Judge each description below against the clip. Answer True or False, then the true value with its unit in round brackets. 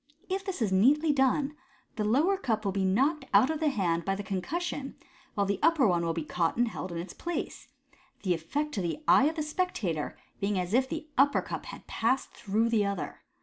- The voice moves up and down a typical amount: False (7.7 semitones)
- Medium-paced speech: False (220 wpm)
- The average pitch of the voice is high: True (230 Hz)